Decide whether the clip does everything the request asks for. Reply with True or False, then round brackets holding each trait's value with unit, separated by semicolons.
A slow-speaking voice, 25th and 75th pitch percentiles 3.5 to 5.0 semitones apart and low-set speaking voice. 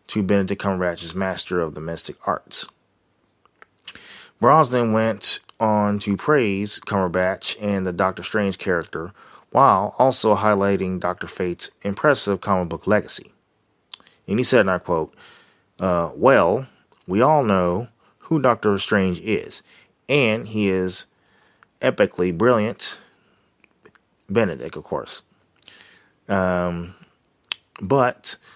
False (110 wpm; 2.7 semitones; 100 Hz)